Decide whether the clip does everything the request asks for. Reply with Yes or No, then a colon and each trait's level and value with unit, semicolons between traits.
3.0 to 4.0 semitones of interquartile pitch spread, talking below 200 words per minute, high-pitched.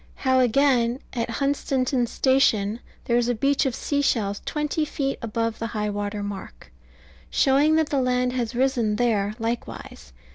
Yes: average, 3.4 semitones; average, 150 wpm; high, 245 Hz